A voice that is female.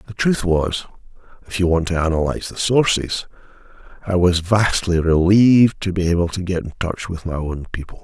No: male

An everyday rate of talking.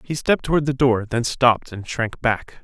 No: fast, 230 wpm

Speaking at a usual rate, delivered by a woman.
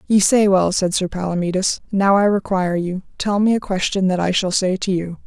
No: fast, 230 wpm; female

